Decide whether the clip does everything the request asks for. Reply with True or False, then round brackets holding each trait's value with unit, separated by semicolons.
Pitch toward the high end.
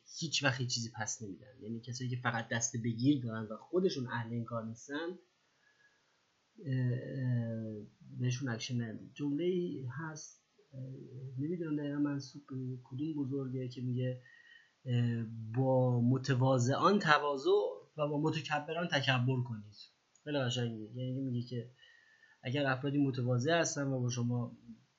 False (130 Hz)